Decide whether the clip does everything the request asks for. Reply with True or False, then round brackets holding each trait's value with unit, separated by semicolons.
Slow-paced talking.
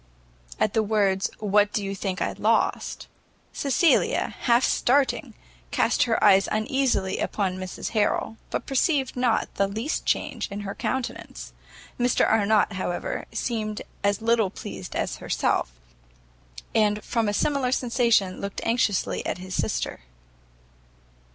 True (130 wpm)